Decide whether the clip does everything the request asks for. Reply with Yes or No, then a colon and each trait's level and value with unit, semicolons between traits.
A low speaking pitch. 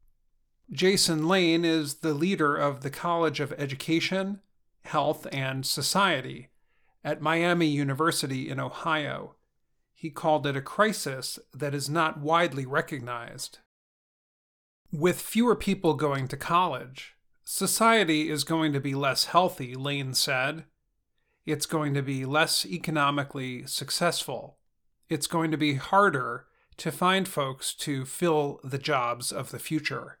No: medium, 155 Hz